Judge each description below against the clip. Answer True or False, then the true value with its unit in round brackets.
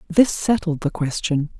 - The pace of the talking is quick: False (150 wpm)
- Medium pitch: True (170 Hz)